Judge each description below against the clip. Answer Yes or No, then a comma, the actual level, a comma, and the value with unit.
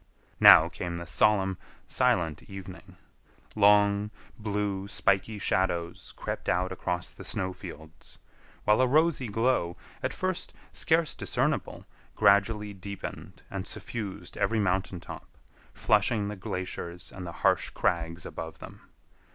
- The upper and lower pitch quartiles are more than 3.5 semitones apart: No, average, 2.8 semitones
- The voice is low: Yes, low, 100 Hz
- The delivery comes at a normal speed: No, slow, 125 wpm